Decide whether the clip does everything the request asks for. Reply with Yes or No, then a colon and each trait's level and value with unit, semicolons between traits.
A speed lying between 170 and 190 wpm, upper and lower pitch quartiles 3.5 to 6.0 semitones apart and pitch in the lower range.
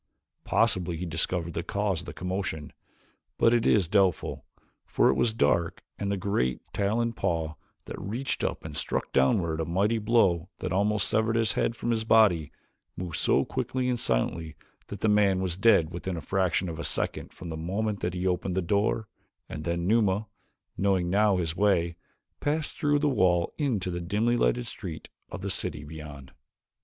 Yes: average, 185 wpm; average, 4.3 semitones; very low, 95 Hz